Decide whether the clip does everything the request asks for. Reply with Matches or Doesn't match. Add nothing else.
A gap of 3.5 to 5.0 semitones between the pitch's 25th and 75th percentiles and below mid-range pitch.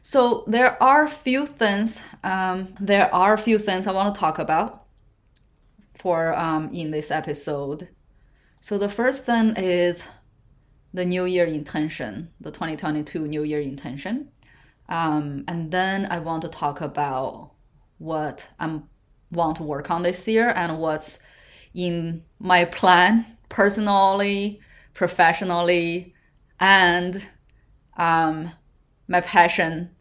Doesn't match